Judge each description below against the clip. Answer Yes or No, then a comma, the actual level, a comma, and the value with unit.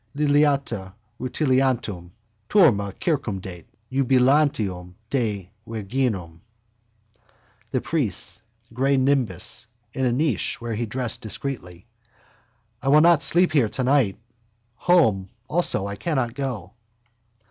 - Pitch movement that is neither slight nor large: No, wide, 5.7 semitones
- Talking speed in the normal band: No, slow, 100 wpm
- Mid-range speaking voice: No, low, 125 Hz